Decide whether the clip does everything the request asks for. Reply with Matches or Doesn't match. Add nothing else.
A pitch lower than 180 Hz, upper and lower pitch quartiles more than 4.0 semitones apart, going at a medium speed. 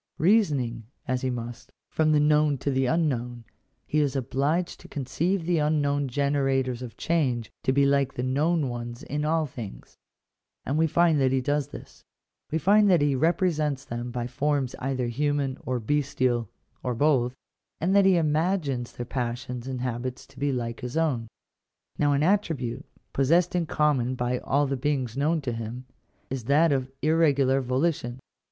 Doesn't match